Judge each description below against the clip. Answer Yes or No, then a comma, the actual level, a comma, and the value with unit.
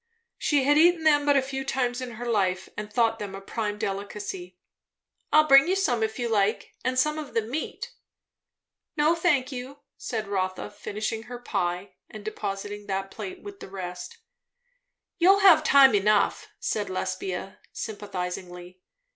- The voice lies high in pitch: Yes, high, 225 Hz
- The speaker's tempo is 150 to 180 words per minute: Yes, average, 160 wpm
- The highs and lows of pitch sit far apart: Yes, wide, 6.1 semitones